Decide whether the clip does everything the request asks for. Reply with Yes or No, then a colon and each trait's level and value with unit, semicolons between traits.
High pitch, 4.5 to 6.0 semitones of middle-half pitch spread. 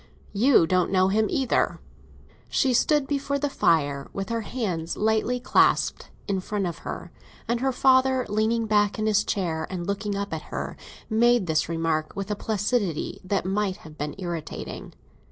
Yes: high, 205 Hz; average, 5.0 semitones